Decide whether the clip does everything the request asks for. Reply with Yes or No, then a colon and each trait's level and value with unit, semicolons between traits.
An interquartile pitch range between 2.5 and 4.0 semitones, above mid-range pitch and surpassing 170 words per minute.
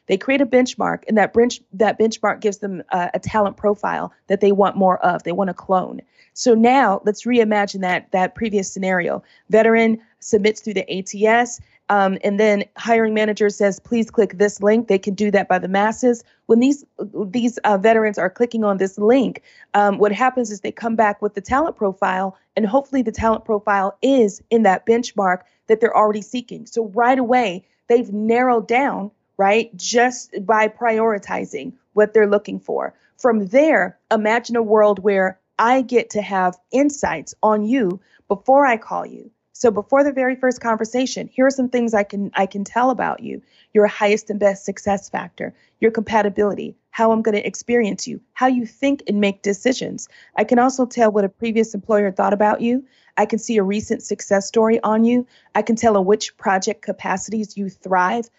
Yes: average, 2.8 semitones; high, 215 Hz; average, 190 wpm